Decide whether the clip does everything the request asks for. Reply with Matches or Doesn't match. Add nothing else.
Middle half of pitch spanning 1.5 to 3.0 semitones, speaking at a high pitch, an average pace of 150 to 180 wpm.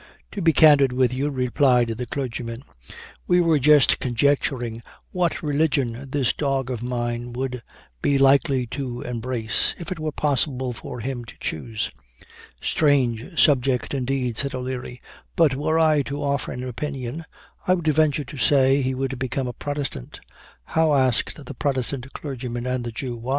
Doesn't match